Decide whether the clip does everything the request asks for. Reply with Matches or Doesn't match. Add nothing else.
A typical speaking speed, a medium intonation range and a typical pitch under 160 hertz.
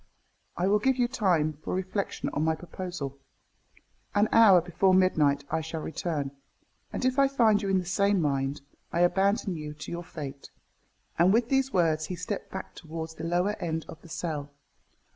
Doesn't match